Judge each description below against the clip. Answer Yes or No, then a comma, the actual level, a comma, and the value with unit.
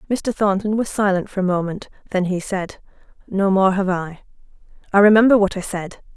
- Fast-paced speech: No, average, 185 wpm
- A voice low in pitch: No, high, 195 Hz